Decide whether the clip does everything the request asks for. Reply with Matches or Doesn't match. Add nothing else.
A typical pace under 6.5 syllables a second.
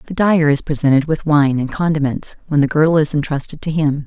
Matches